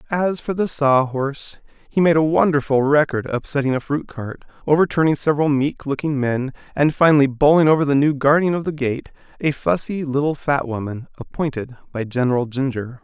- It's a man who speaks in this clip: Yes, male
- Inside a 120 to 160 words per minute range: No, average, 170 wpm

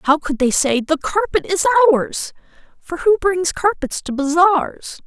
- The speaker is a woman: Yes, female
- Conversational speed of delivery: Yes, average, 165 wpm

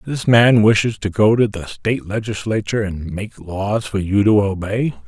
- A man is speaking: Yes, male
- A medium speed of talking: Yes, average, 190 wpm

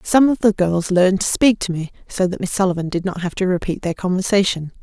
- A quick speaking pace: Yes, fast, 250 wpm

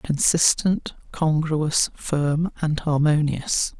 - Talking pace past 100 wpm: No, slow, 80 wpm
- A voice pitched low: No, medium, 155 Hz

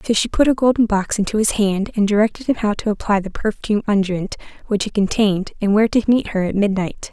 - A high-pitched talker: Yes, high, 210 Hz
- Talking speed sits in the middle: No, fast, 235 wpm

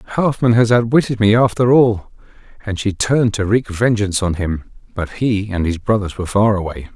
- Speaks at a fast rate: No, average, 190 wpm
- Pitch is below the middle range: Yes, low, 105 Hz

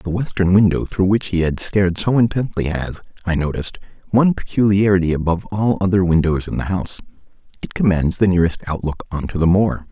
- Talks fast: No, average, 180 wpm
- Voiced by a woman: No, male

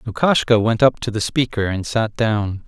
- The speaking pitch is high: No, low, 115 Hz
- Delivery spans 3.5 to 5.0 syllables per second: Yes, 4.7 syllables/s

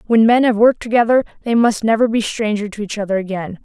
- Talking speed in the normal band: No, fast, 230 wpm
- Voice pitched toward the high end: Yes, high, 220 Hz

